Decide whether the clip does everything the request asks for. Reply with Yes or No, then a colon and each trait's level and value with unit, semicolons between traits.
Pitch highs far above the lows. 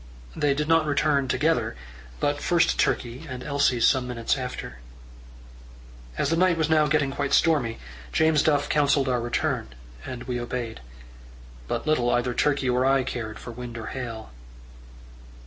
No: average, 3.6 semitones